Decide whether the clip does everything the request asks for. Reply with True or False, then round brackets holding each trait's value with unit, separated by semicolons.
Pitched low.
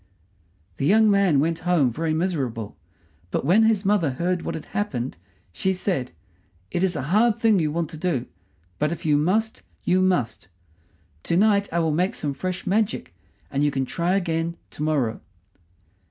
False (170 Hz)